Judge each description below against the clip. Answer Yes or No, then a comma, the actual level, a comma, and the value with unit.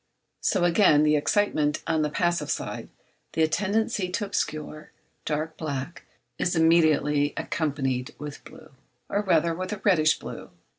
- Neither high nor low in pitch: Yes, medium, 160 Hz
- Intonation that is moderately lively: Yes, average, 3.4 semitones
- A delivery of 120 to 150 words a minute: Yes, average, 140 wpm